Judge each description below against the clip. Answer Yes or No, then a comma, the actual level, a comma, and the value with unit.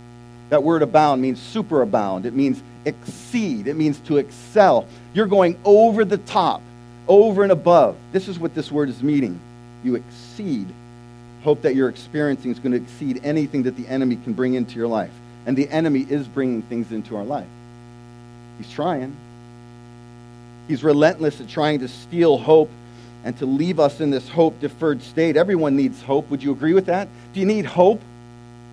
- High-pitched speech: No, low, 135 Hz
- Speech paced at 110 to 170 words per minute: No, average, 180 wpm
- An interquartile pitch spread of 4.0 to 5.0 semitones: Yes, average, 4.3 semitones